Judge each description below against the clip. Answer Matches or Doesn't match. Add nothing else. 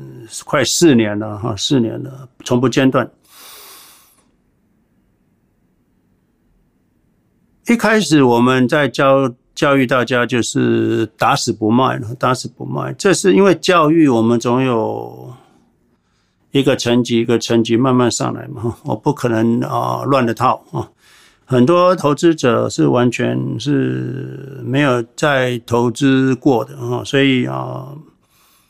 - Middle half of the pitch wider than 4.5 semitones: Doesn't match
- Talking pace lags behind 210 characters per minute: Matches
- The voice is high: Doesn't match